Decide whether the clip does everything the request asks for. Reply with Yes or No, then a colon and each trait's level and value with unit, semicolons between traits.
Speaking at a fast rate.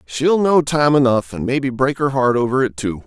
Yes: fast, 235 wpm